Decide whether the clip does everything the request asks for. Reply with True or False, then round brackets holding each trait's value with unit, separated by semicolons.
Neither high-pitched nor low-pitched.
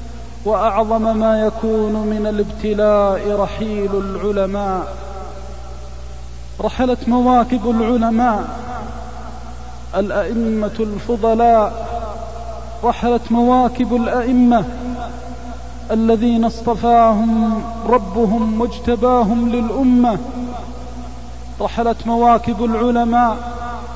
False (225 Hz)